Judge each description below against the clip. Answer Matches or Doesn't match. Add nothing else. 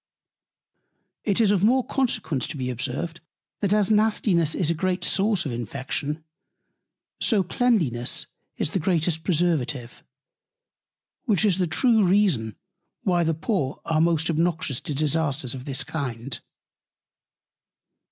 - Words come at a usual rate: Doesn't match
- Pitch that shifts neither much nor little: Doesn't match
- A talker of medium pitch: Matches